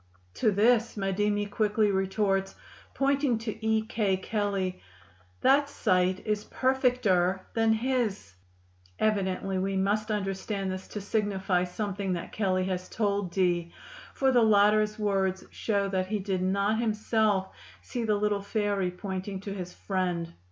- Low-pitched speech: No, high, 200 Hz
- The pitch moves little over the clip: Yes, narrow, 2.3 semitones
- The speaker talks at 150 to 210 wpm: No, slow, 135 wpm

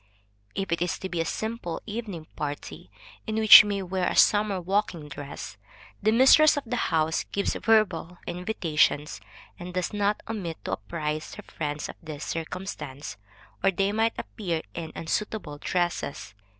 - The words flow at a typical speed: Yes, average, 160 wpm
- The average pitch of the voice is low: No, medium, 180 Hz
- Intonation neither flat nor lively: Yes, average, 4.7 semitones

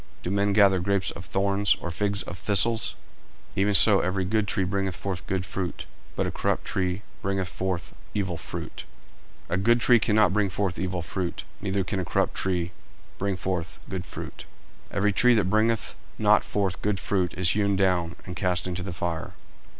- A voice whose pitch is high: No, very low, 95 Hz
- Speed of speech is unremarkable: Yes, average, 190 wpm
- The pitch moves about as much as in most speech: No, narrow, 1.9 semitones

